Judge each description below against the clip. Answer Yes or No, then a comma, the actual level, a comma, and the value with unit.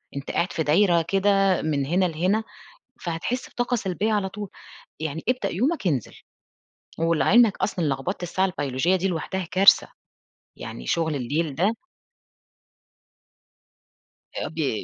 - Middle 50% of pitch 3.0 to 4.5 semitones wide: Yes, average, 4.0 semitones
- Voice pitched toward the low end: No, medium, 180 Hz